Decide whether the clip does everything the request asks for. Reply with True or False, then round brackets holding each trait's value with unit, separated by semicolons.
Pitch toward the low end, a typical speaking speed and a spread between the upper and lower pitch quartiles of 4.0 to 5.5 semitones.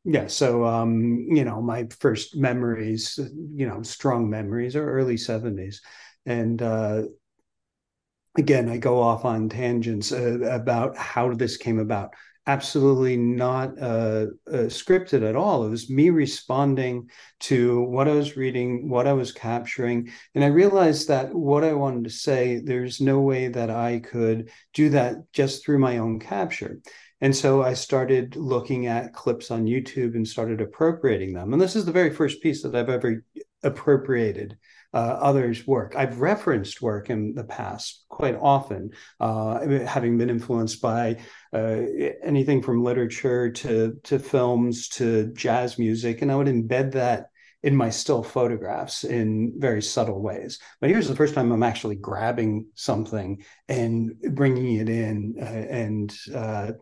False (120 Hz; 160 wpm; 3.1 semitones)